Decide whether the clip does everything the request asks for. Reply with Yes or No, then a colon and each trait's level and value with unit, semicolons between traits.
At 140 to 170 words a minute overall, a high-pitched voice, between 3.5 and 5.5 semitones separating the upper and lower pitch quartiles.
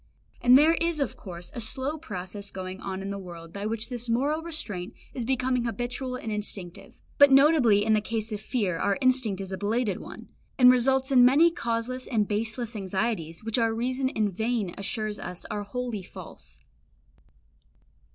No: average, 180 wpm; high, 225 Hz; average, 4.1 semitones